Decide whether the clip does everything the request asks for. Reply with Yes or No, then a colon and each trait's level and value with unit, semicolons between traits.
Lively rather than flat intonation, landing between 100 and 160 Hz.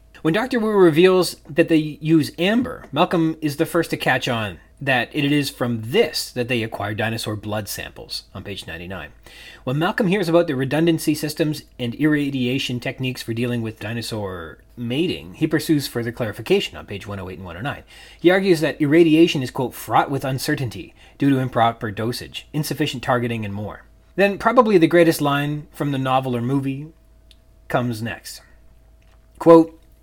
Yes: wide, 5.7 semitones; low, 135 Hz